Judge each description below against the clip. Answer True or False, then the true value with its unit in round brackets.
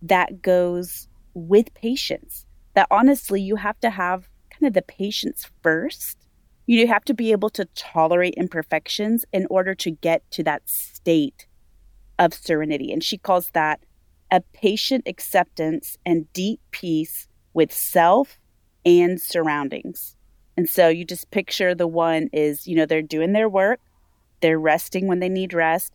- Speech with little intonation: False (3.6 semitones)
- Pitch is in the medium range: True (175 Hz)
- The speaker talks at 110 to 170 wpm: True (155 wpm)